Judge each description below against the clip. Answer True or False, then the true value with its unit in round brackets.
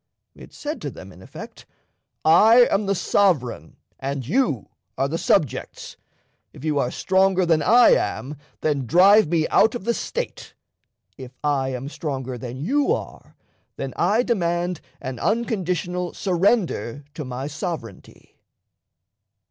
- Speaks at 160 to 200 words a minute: False (140 wpm)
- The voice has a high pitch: False (170 Hz)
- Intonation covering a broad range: True (6.8 semitones)